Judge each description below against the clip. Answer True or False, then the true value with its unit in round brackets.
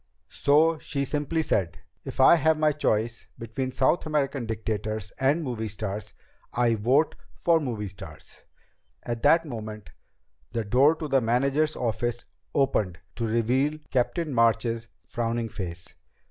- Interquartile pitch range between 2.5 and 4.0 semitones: False (4.7 semitones)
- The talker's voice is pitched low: True (120 Hz)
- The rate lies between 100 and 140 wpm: True (135 wpm)